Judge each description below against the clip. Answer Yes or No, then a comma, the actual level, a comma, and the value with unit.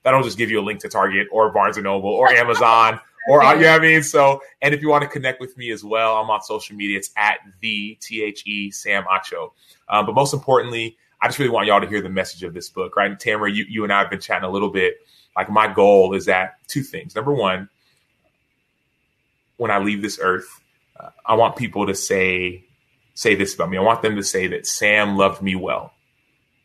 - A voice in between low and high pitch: No, low, 110 Hz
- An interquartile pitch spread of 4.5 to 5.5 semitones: Yes, average, 5.2 semitones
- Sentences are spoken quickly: Yes, fast, 240 wpm